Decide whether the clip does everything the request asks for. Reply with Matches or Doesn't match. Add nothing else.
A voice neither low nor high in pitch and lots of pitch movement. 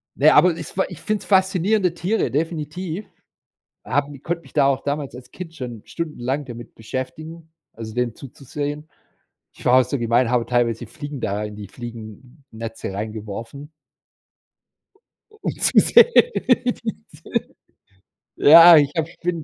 Matches